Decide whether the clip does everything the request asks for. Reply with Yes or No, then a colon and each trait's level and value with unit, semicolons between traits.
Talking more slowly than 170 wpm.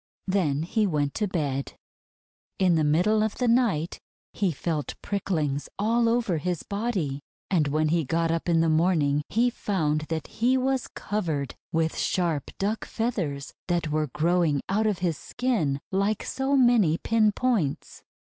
Yes: average, 160 wpm